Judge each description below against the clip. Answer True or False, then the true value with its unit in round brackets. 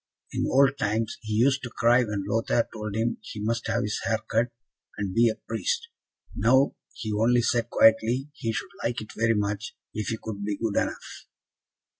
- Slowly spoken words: False (190 wpm)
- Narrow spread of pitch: True (1.9 semitones)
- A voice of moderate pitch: False (115 Hz)